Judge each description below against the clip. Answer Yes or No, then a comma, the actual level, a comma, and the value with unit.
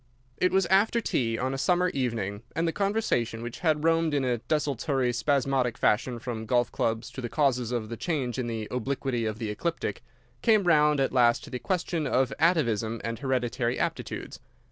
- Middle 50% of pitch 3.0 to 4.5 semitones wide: No, average, 5.0 semitones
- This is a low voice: Yes, low, 130 Hz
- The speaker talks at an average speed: Yes, average, 190 wpm